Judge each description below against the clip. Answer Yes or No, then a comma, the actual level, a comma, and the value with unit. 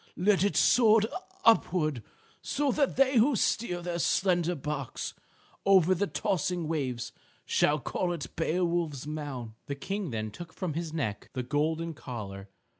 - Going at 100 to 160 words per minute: Yes, average, 145 wpm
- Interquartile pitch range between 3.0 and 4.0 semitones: No, average, 4.7 semitones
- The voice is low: No, medium, 165 Hz